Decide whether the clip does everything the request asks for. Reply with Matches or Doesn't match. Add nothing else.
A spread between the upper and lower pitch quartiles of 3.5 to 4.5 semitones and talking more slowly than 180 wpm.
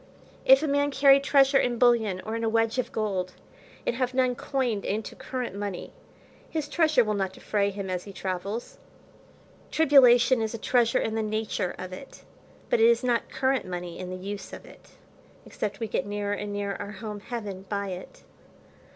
Doesn't match